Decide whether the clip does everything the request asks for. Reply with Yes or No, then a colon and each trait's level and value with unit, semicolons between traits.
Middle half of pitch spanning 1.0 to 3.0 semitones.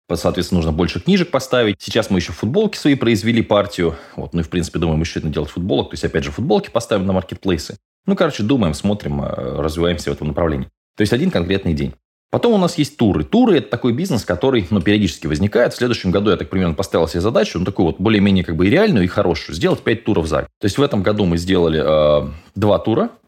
No: average, 4.0 semitones